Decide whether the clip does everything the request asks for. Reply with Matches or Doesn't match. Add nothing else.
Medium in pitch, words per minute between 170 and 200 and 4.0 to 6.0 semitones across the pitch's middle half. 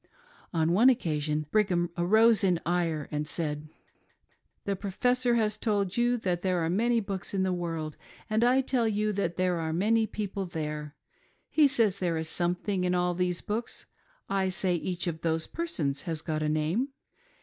Matches